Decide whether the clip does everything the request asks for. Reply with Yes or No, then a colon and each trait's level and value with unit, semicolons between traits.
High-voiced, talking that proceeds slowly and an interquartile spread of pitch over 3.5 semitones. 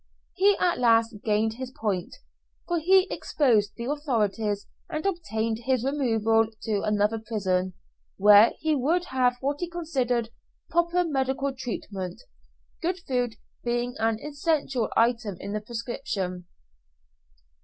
Yes: high, 240 Hz; slow, 125 wpm; average, 5.0 semitones